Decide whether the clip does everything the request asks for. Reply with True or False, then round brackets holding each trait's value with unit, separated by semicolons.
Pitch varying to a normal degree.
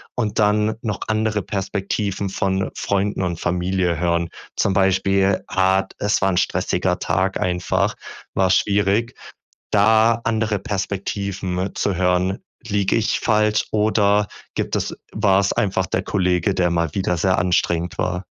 False (2.2 semitones)